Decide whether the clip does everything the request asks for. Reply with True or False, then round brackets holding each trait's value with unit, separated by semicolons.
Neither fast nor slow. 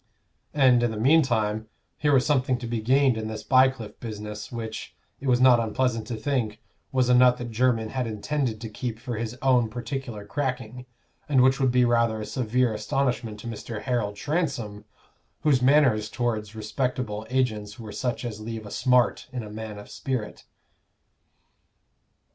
True (170 wpm)